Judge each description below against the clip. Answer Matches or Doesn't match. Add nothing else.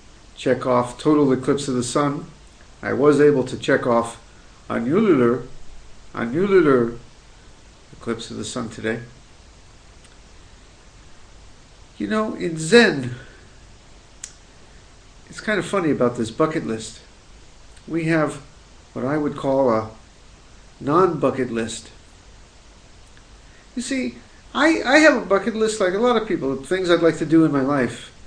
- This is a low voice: Matches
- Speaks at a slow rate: Matches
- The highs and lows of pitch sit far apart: Matches